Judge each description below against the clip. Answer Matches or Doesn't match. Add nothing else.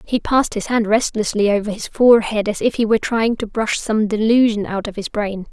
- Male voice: Doesn't match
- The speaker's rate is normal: Doesn't match